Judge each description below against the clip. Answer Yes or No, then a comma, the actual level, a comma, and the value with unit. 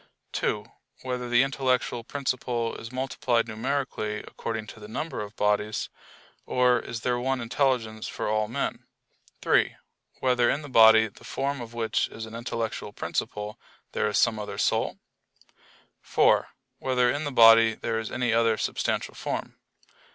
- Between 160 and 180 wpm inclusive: No, average, 150 wpm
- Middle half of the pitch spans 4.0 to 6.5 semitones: No, narrow, 2.4 semitones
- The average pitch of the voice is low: Yes, low, 115 Hz